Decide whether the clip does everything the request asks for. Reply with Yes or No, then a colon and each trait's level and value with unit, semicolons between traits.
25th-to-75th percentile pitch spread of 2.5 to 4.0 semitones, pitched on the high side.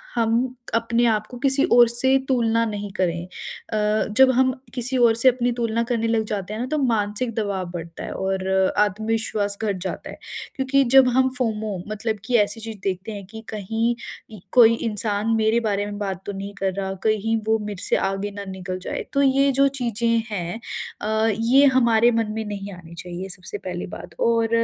Yes: average, 2.8 semitones; high, 220 Hz